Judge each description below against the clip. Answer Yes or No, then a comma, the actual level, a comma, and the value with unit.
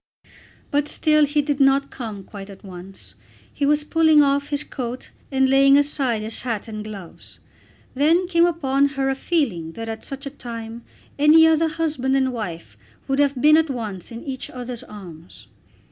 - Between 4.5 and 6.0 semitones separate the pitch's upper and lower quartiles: Yes, average, 4.8 semitones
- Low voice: No, very high, 270 Hz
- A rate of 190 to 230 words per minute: No, average, 175 wpm